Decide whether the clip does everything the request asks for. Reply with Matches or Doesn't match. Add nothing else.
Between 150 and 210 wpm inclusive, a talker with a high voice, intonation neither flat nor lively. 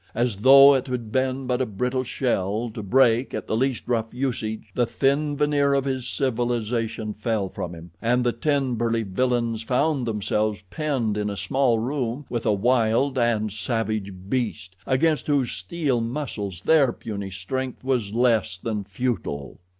Doesn't match